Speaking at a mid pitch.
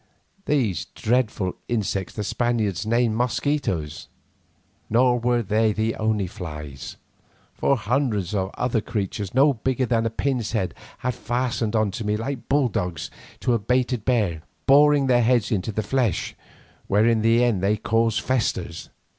No: low, 115 Hz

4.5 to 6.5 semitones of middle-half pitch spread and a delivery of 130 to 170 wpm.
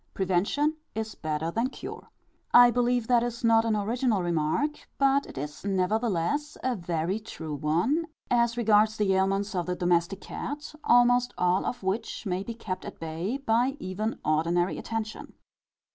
Yes: average, 5.2 semitones; average, 160 wpm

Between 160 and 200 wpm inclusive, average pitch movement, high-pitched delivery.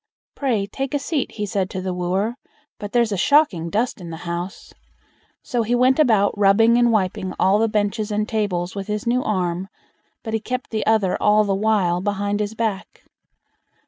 Yes: average, 190 wpm; average, 3.1 semitones; high, 210 Hz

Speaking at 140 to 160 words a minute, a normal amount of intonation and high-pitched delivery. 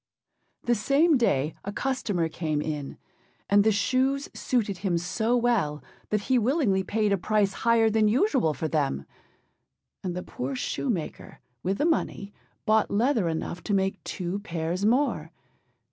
No: average, 150 wpm; wide, 5.8 semitones; high, 205 Hz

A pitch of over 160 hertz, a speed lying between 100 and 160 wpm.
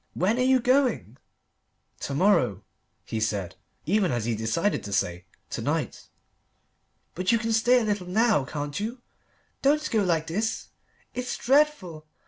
Yes: high, 190 Hz; average, 150 wpm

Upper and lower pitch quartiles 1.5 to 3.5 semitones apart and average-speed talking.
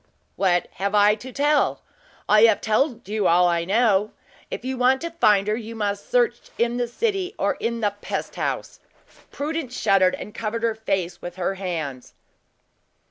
No: average, 4.3 semitones; average, 175 wpm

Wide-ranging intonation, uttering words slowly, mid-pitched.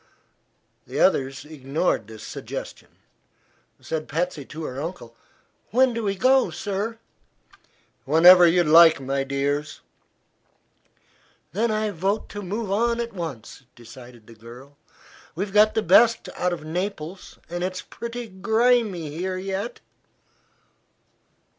Yes: wide, 6.4 semitones; slow, 120 wpm; medium, 180 Hz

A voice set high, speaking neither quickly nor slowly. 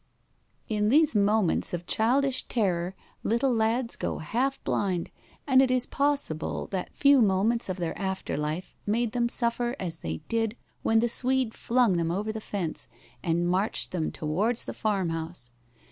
Yes: high, 215 Hz; average, 160 wpm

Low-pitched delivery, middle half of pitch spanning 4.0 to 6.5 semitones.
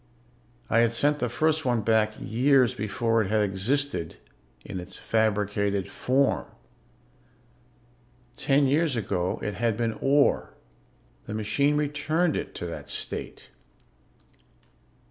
Yes: low, 115 Hz; wide, 5.4 semitones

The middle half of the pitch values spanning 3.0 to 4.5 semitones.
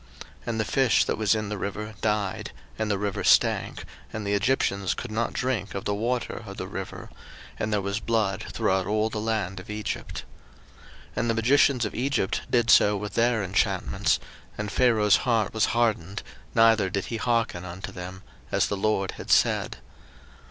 No: narrow, 2.6 semitones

